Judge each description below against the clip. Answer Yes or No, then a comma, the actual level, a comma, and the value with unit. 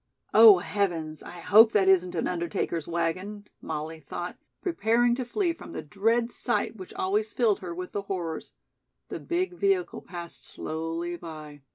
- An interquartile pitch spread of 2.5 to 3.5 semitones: No, average, 5.0 semitones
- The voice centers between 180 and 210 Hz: Yes, medium, 185 Hz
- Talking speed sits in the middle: Yes, average, 160 wpm